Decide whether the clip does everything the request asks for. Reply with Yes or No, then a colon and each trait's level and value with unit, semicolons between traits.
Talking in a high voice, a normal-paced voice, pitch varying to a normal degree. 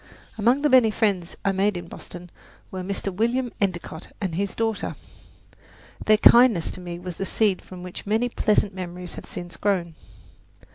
Yes: high, 195 Hz; average, 170 wpm; average, 3.6 semitones